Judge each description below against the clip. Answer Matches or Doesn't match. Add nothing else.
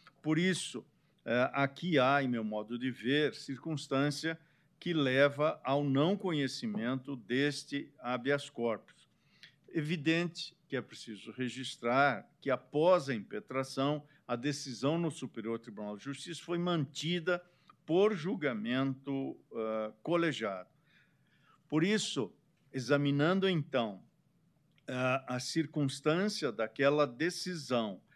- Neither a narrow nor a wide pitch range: Matches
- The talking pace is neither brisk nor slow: Doesn't match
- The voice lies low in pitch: Doesn't match